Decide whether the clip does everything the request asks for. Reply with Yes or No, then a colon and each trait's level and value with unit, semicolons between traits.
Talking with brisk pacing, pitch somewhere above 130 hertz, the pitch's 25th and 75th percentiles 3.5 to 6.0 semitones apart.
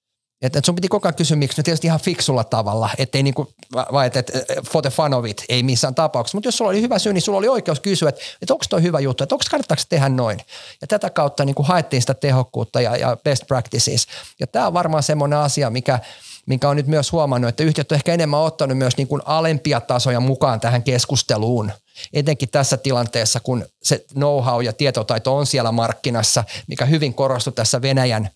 Yes: fast, 205 wpm; medium, 140 Hz; average, 3.8 semitones